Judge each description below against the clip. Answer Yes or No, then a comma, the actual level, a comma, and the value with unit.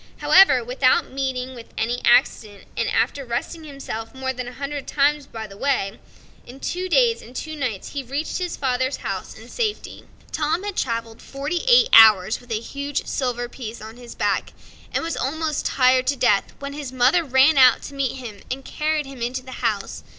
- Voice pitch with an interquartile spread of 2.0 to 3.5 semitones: Yes, average, 3.2 semitones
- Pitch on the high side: Yes, very high, 260 Hz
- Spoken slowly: No, average, 190 wpm